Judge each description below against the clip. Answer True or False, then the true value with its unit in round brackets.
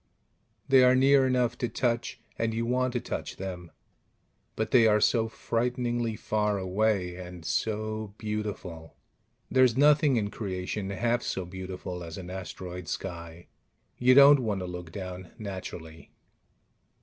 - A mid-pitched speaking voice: False (105 Hz)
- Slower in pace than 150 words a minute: True (140 wpm)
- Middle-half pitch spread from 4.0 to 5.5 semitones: True (4.7 semitones)